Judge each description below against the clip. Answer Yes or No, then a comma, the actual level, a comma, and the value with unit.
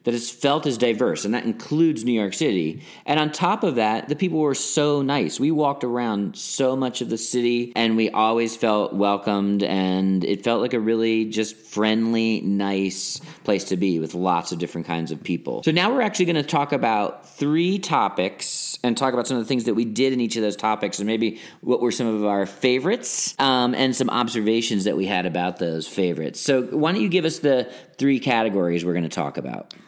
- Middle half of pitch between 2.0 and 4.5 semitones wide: No, average, 5.3 semitones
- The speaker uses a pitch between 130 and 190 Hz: No, low, 115 Hz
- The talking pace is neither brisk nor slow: No, fast, 215 wpm